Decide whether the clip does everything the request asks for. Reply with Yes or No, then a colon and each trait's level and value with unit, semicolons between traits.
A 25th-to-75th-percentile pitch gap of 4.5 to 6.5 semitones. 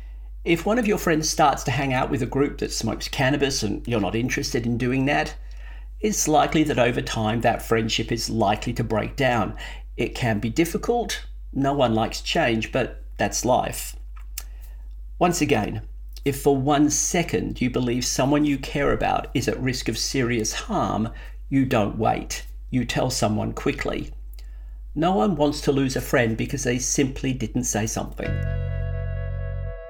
Yes: average, 5.2 semitones